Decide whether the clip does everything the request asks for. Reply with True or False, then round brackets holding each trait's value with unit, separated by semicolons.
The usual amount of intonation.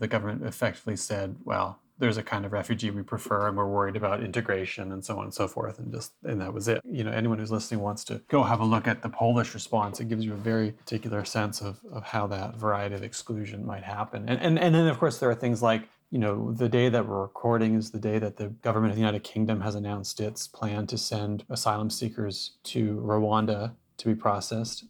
False (1.9 semitones)